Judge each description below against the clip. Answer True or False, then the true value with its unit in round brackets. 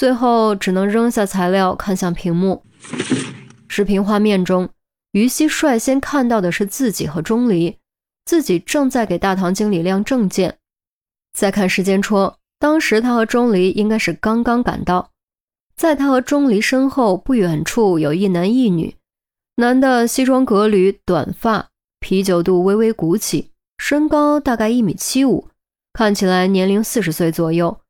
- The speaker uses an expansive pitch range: False (4.6 semitones)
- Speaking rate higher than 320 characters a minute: False (230 characters per minute)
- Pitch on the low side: False (210 Hz)